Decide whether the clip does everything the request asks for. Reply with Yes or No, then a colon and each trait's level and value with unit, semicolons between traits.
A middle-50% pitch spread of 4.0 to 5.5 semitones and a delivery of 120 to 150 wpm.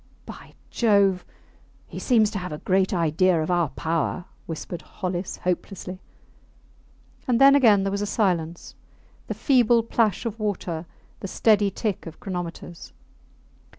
No: average, 3.6 semitones; average, 140 wpm